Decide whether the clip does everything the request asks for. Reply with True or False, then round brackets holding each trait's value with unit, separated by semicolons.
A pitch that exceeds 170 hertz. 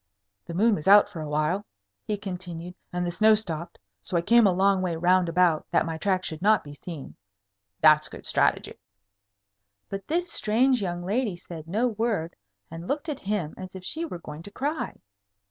True (185 Hz)